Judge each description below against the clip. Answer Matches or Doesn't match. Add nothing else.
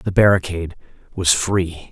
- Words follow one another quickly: Doesn't match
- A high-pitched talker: Doesn't match